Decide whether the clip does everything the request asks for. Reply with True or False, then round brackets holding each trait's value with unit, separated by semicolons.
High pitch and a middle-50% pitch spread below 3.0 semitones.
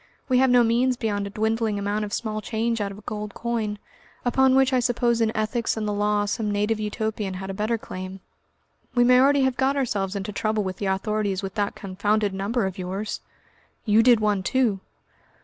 True (215 Hz; 2.6 semitones)